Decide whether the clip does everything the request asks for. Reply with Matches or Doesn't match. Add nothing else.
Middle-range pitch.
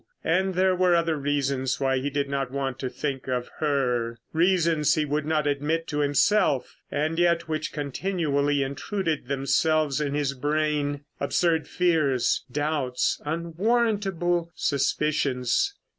Matches